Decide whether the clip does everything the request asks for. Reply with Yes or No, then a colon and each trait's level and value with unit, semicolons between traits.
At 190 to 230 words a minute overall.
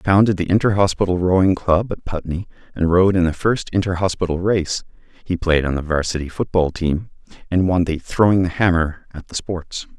Yes: average, 200 wpm